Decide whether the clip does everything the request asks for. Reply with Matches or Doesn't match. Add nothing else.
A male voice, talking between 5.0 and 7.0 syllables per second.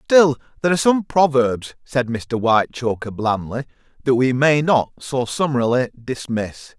Doesn't match